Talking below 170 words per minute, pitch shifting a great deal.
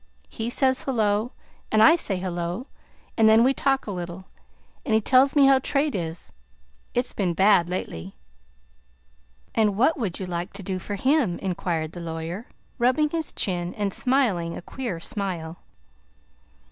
Yes: average, 160 wpm; wide, 6.4 semitones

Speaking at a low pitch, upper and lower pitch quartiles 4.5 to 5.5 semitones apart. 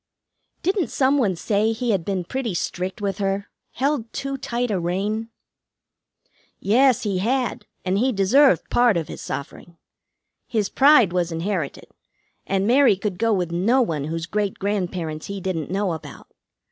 No: high, 200 Hz; average, 4.9 semitones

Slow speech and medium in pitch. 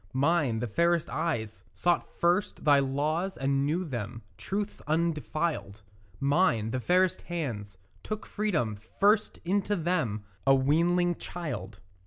Yes: slow, 125 wpm; medium, 155 Hz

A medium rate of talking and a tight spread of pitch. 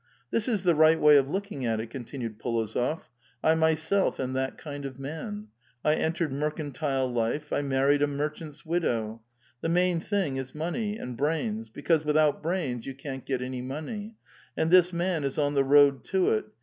No: average, 185 wpm; average, 4.0 semitones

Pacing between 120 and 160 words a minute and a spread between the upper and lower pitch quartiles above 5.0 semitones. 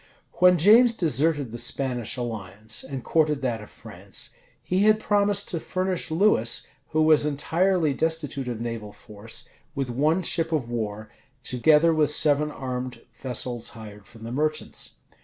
Yes: average, 150 wpm; wide, 5.6 semitones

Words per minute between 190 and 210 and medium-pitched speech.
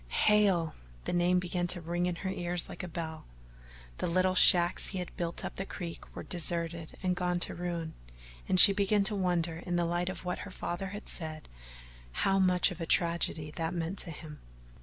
Yes: average, 200 wpm; medium, 175 Hz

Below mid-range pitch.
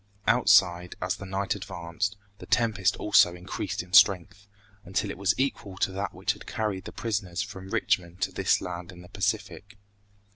Yes: very low, 95 Hz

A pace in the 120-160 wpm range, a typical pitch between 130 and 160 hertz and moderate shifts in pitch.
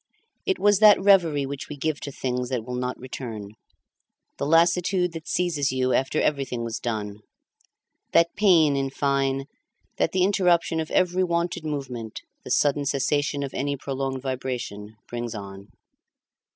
Yes: average, 150 wpm; medium, 140 Hz; average, 4.9 semitones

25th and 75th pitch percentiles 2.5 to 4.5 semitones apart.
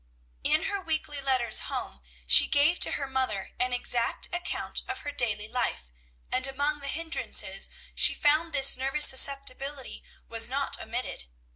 Yes: average, 3.2 semitones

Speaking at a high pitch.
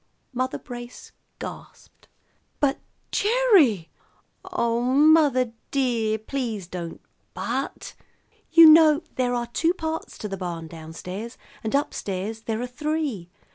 Yes: high, 245 Hz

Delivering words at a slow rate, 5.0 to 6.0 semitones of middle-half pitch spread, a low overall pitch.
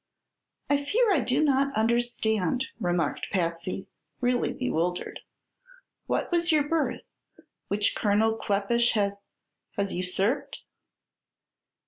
No: slow, 100 wpm; wide, 5.4 semitones; high, 225 Hz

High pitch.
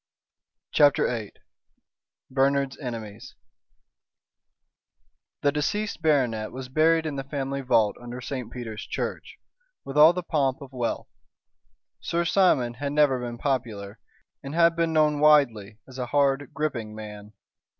No: low, 135 Hz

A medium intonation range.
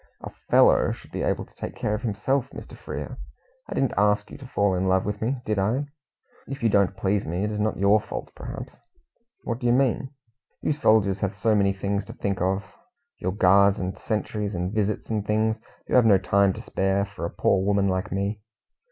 No: narrow, 2.1 semitones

